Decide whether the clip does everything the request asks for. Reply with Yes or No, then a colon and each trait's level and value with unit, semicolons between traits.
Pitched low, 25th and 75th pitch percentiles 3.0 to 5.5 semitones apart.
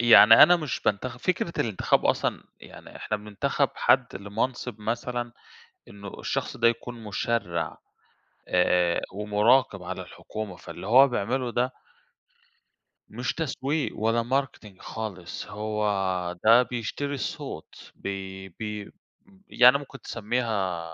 Yes: low, 115 Hz; average, 3.7 semitones